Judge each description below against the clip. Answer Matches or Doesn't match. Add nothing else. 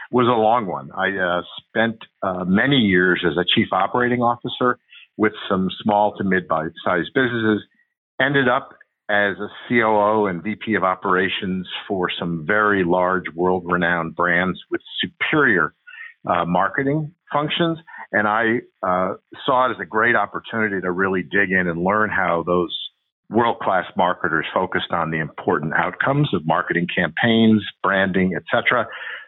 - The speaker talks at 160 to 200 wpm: Doesn't match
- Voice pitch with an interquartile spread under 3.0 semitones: Doesn't match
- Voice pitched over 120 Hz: Doesn't match